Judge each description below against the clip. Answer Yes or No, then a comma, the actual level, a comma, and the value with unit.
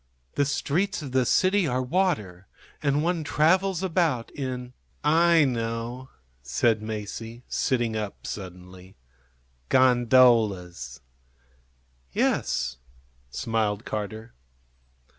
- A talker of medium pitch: No, low, 120 Hz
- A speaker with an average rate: No, slow, 95 wpm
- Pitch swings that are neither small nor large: No, wide, 5.8 semitones